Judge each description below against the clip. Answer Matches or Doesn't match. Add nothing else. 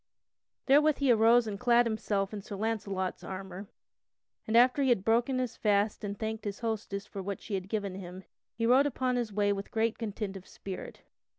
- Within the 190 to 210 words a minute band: Matches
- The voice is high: Matches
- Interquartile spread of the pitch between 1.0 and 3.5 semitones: Matches